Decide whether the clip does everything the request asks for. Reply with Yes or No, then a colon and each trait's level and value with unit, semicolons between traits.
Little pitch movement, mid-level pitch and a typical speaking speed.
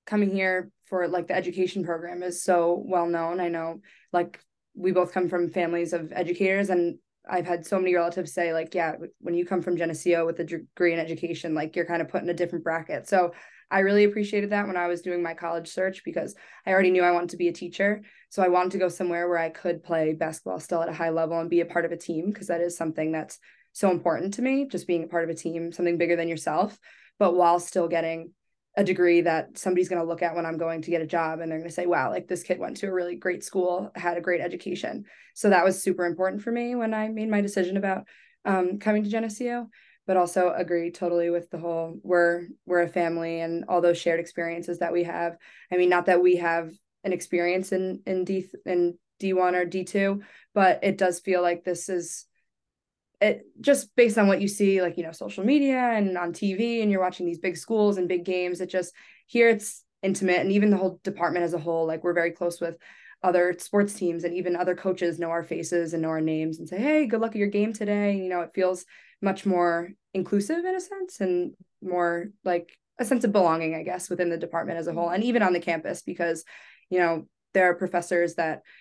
No: narrow, 1.9 semitones; medium, 180 Hz; fast, 240 wpm